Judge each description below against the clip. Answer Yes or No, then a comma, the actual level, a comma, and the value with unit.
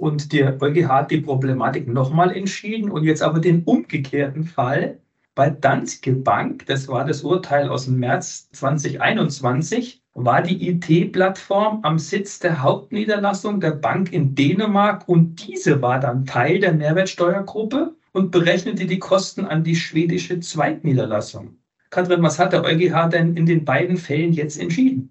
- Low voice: No, medium, 165 Hz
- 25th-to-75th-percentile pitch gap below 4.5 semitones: No, average, 4.8 semitones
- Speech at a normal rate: Yes, average, 150 wpm